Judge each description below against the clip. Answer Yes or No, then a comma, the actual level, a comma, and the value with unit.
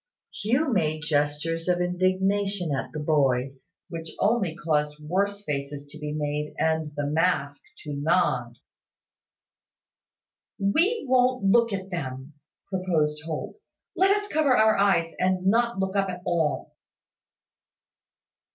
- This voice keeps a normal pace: No, slow, 125 wpm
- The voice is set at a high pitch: No, medium, 175 Hz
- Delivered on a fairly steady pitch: No, average, 5.0 semitones